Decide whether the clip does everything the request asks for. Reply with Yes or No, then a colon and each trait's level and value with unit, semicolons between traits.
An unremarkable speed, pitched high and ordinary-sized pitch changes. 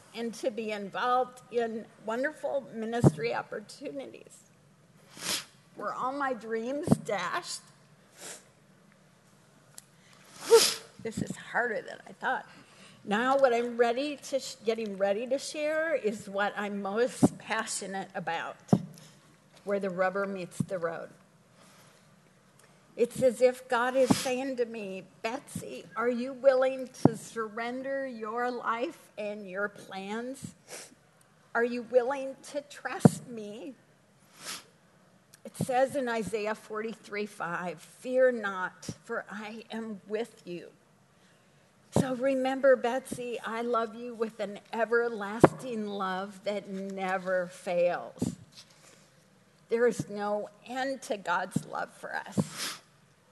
No: slow, 115 wpm; high, 225 Hz; average, 4.7 semitones